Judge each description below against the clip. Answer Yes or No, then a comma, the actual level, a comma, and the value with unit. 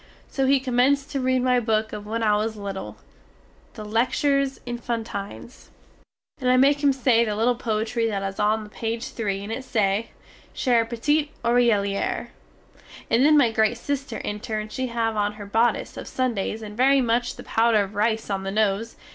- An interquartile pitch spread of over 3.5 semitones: No, average, 3.1 semitones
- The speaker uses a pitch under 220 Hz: No, high, 230 Hz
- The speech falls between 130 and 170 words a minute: No, average, 185 wpm